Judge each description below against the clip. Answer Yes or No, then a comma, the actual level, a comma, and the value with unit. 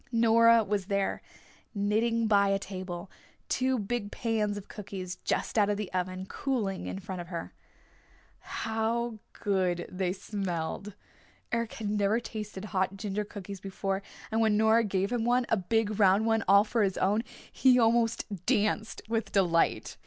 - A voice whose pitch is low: No, high, 205 Hz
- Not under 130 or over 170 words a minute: Yes, average, 160 wpm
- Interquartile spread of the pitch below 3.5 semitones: Yes, average, 2.7 semitones